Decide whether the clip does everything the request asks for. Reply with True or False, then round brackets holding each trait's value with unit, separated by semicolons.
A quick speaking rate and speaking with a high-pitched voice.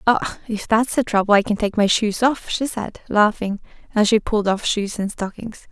True (220 wpm; 215 Hz)